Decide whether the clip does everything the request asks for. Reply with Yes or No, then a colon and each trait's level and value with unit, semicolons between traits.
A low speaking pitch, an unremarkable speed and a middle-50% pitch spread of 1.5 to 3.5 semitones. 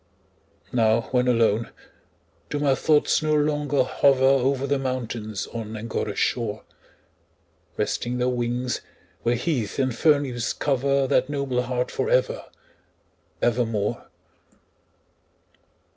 No: low, 125 Hz; slow, 115 wpm; average, 3.0 semitones